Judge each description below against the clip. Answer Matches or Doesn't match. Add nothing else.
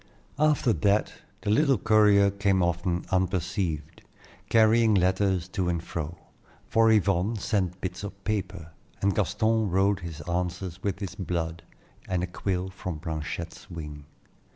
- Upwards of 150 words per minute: Doesn't match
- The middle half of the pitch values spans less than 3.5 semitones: Matches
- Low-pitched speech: Matches